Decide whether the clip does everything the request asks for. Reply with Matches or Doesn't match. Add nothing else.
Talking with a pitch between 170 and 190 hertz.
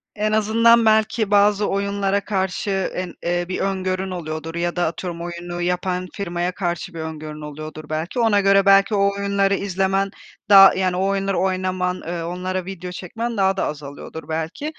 Matches